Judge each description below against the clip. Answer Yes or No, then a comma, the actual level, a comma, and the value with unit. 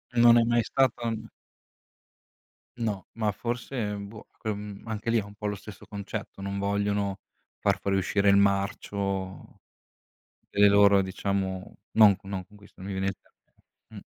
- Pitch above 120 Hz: No, low, 100 Hz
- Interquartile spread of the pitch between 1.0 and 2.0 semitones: Yes, narrow, 1.6 semitones